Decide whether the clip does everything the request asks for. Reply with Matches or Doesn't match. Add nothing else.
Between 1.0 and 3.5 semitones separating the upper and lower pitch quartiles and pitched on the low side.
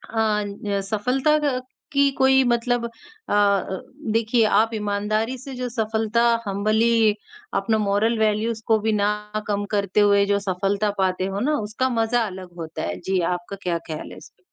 Doesn't match